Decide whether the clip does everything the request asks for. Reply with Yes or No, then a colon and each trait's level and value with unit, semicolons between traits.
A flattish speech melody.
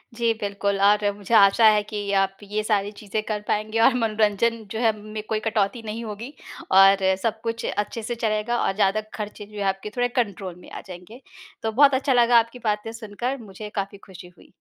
Yes: narrow, 2.2 semitones